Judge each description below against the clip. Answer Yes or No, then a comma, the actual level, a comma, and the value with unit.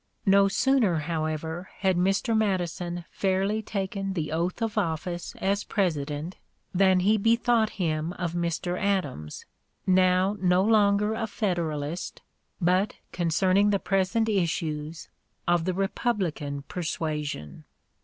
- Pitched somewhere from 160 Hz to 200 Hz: Yes, medium, 185 Hz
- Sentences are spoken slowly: Yes, slow, 115 wpm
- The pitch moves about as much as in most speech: Yes, average, 3.5 semitones